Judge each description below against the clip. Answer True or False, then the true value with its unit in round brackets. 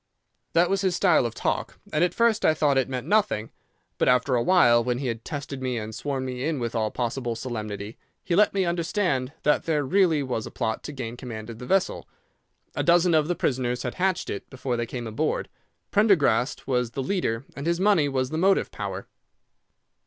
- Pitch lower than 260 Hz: True (135 Hz)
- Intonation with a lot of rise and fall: True (6.3 semitones)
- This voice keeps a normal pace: False (210 wpm)